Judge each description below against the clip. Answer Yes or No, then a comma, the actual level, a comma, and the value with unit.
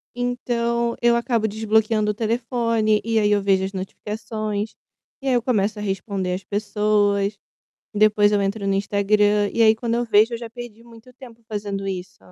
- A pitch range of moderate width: No, narrow, 2.3 semitones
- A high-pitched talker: Yes, high, 215 Hz